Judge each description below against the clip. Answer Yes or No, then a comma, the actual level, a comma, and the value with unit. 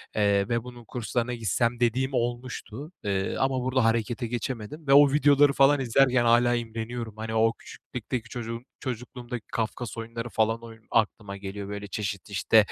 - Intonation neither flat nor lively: No, narrow, 2.2 semitones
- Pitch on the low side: Yes, low, 120 Hz